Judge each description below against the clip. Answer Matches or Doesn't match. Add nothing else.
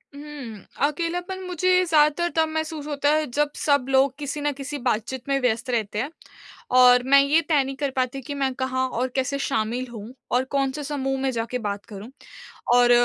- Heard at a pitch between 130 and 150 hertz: Doesn't match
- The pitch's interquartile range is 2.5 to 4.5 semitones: Matches